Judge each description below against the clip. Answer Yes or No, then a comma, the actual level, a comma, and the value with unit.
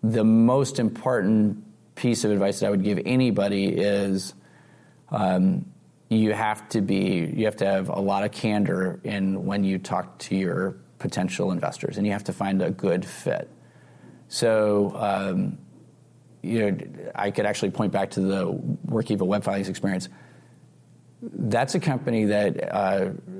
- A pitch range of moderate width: Yes, average, 3.3 semitones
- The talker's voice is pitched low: Yes, low, 105 Hz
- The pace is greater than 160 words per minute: No, average, 155 wpm